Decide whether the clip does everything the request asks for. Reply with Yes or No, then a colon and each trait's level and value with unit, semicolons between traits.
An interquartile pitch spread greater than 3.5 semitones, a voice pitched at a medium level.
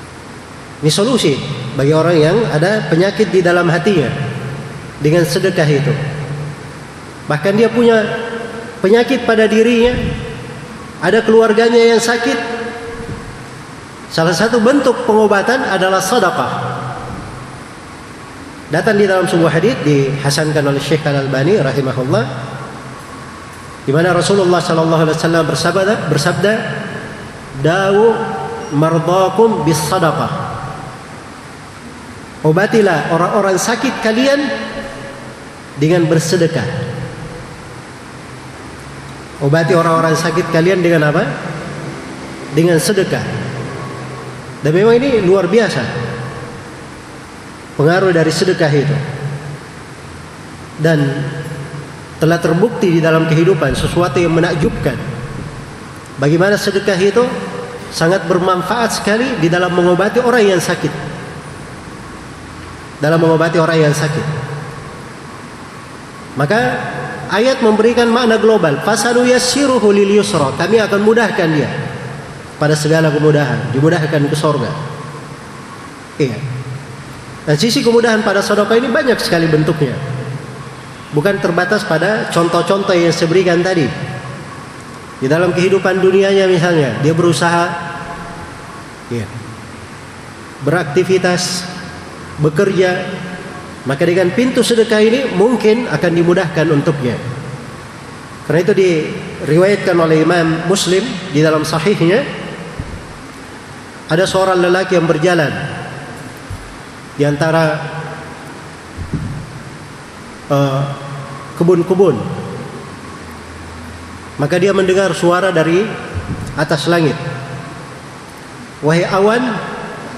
Yes: average, 4.9 semitones; medium, 165 Hz